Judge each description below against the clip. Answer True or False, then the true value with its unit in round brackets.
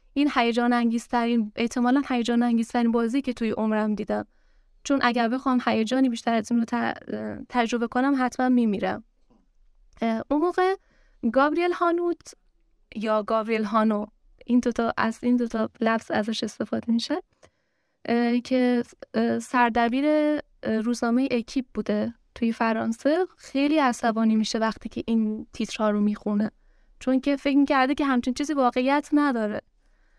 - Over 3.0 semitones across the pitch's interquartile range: False (2.7 semitones)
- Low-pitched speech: False (240 Hz)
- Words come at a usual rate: True (130 wpm)